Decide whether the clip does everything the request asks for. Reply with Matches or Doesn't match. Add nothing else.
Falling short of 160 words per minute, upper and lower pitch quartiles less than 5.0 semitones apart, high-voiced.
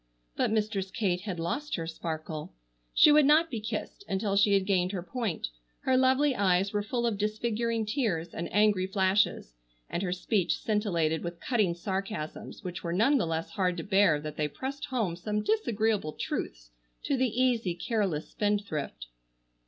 Doesn't match